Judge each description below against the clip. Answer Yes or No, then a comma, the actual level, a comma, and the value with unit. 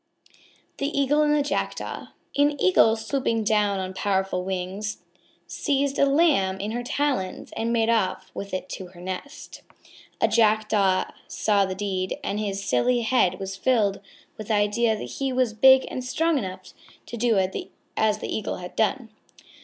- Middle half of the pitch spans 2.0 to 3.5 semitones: No, average, 5.0 semitones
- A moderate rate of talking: Yes, average, 170 wpm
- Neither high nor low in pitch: No, high, 215 Hz